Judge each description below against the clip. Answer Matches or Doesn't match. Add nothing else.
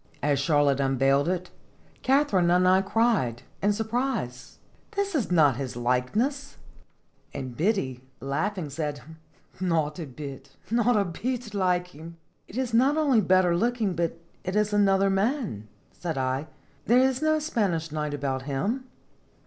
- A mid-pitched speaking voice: Matches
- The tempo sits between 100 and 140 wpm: Doesn't match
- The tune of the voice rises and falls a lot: Matches